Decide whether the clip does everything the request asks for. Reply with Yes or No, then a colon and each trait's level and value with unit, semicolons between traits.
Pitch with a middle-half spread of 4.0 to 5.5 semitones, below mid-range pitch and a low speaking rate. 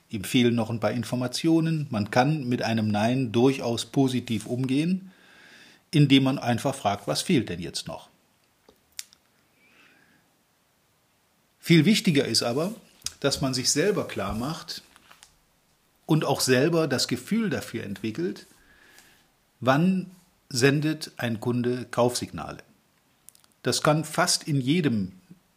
Yes: average, 5.0 semitones; low, 130 Hz; slow, 115 wpm